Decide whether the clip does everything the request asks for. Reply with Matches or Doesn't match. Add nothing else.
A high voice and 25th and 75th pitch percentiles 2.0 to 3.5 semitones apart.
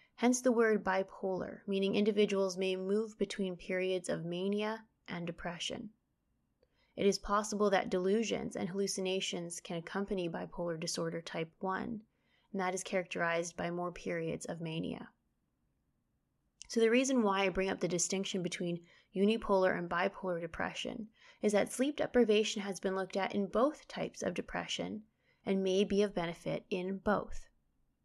Matches